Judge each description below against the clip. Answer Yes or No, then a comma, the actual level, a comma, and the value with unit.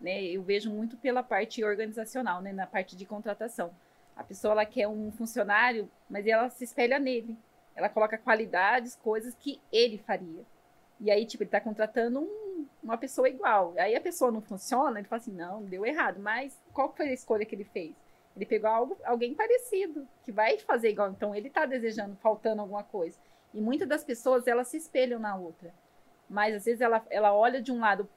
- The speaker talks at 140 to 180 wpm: No, average, 200 wpm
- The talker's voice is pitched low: No, high, 225 Hz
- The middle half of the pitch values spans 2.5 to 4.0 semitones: Yes, average, 3.6 semitones